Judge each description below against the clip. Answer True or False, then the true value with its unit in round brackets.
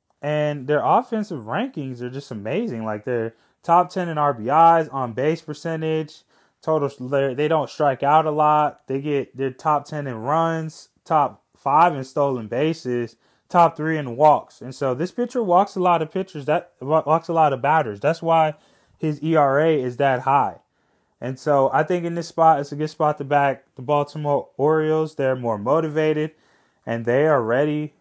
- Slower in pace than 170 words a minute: False (180 wpm)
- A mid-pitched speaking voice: True (150 Hz)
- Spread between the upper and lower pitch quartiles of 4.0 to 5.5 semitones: False (2.8 semitones)